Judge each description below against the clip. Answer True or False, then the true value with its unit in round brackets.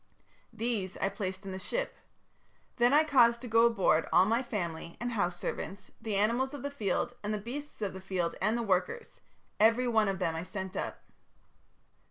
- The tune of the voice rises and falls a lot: False (4.1 semitones)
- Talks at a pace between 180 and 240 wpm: True (195 wpm)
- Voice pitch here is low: False (215 Hz)